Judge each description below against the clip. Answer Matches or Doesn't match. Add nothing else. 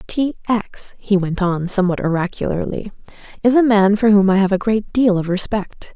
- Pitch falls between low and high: Doesn't match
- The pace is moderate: Matches